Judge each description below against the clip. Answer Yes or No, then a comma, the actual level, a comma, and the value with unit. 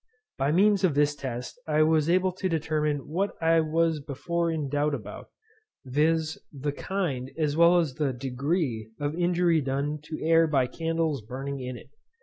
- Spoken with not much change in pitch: No, average, 3.1 semitones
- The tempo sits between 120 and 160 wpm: No, average, 170 wpm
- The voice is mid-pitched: Yes, medium, 155 Hz